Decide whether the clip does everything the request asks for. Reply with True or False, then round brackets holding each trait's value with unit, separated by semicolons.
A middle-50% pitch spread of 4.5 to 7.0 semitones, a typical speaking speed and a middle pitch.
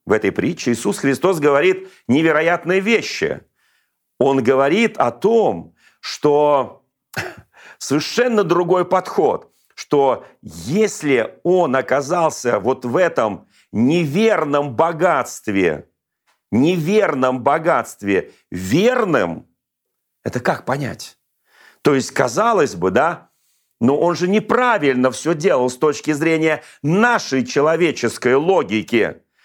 False (5.5 semitones; 100 wpm; 160 Hz)